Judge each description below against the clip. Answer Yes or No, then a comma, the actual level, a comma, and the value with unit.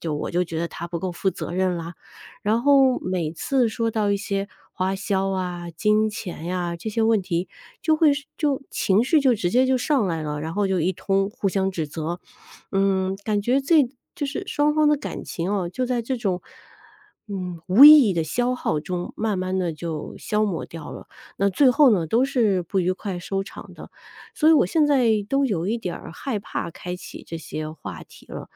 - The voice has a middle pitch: No, high, 195 Hz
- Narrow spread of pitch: No, wide, 5.5 semitones